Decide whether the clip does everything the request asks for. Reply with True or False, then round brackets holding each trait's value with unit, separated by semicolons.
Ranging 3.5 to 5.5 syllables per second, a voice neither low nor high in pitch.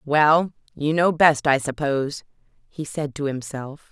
True (4.2 syllables/s; 145 Hz)